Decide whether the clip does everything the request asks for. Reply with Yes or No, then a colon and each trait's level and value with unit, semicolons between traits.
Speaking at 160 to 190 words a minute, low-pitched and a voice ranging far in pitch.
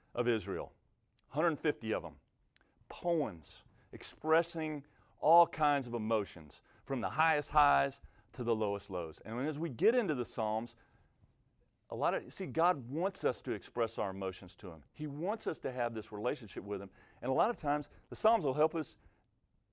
Yes: average, 180 wpm; low, 120 Hz; wide, 7.0 semitones